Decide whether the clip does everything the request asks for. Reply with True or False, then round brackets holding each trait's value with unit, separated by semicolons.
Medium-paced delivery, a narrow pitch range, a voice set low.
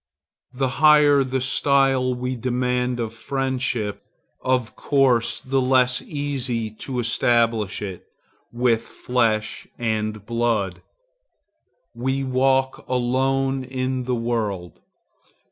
False (100 wpm; 2.3 semitones; 125 Hz)